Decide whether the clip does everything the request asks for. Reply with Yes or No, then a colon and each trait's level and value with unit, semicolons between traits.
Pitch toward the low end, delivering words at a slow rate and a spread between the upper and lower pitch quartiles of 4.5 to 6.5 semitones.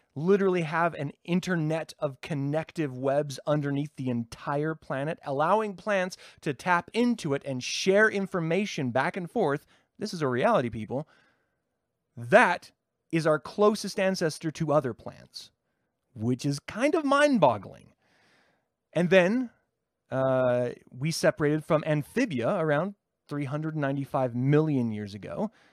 No: medium, 155 Hz; slow, 125 wpm; wide, 5.6 semitones